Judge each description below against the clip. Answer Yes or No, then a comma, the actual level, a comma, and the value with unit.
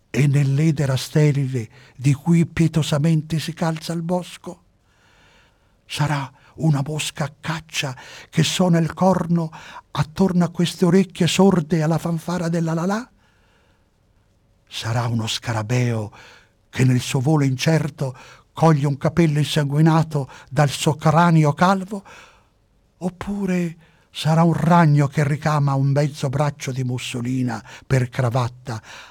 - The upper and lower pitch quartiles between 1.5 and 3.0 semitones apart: No, average, 4.6 semitones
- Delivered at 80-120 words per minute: Yes, slow, 115 wpm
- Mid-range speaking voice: Yes, medium, 150 Hz